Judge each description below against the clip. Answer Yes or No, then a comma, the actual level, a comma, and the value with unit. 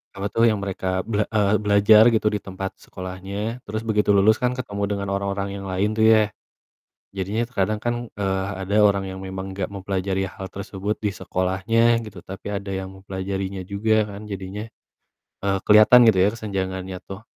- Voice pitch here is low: Yes, low, 100 Hz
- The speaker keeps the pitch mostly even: Yes, narrow, 1.7 semitones